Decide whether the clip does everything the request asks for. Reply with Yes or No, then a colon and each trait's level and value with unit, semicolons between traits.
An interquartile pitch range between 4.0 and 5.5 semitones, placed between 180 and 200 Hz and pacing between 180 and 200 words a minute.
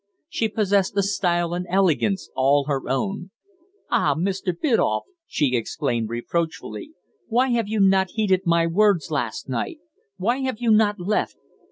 No: average, 5.1 semitones; high, 190 Hz; average, 150 wpm